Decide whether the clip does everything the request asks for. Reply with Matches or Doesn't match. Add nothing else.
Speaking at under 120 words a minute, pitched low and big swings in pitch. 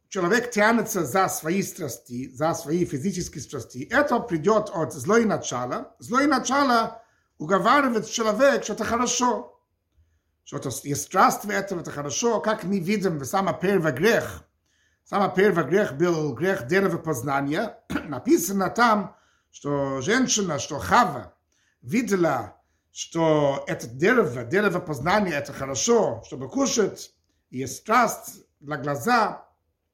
Doesn't match